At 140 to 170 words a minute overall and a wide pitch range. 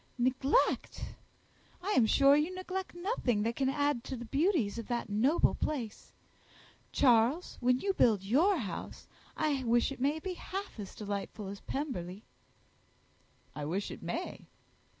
Yes: average, 150 wpm; wide, 5.9 semitones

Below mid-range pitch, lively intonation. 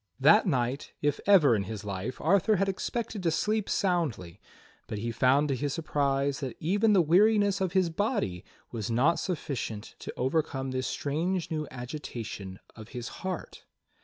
No: medium, 145 Hz; wide, 7.4 semitones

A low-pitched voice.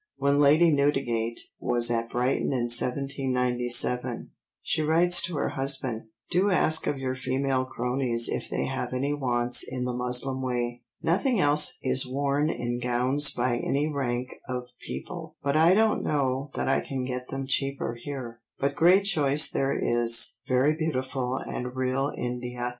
Yes: low, 130 Hz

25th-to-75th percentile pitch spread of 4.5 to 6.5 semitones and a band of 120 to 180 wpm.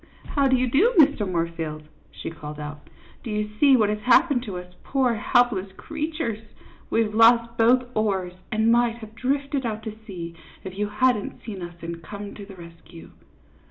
No: average, 5.1 semitones; average, 190 wpm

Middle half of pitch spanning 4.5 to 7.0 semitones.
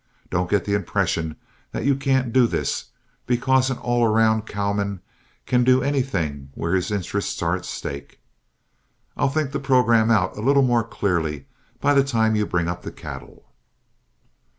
Yes: wide, 5.4 semitones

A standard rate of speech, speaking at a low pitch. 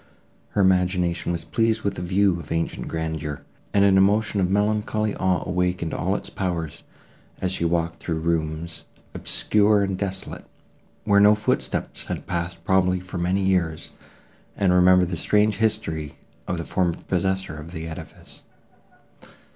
Yes: average, 150 wpm; very low, 90 Hz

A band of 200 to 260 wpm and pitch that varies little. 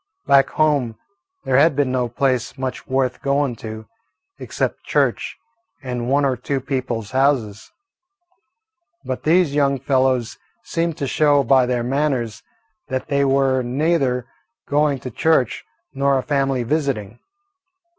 No: slow, 135 wpm; narrow, 2.2 semitones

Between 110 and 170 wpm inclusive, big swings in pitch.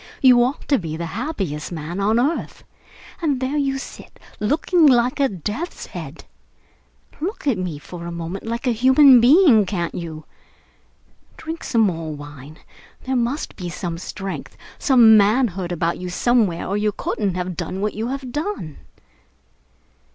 Yes: average, 160 wpm; wide, 7.2 semitones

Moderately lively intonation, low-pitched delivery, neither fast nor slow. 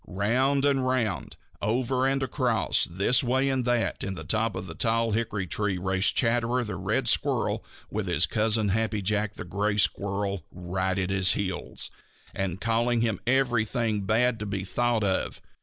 Yes: average, 3.8 semitones; low, 110 Hz; average, 175 wpm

